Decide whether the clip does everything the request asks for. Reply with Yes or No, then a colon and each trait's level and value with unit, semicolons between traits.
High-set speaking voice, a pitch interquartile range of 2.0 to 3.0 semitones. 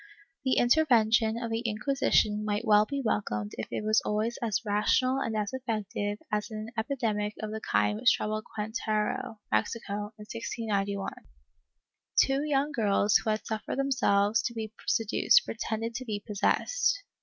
Yes: high, 220 Hz; narrow, 2.4 semitones